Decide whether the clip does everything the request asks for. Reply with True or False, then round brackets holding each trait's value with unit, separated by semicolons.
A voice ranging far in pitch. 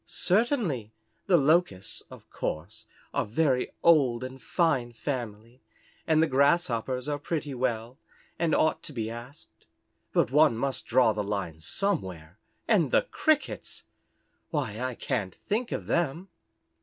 True (6.2 semitones)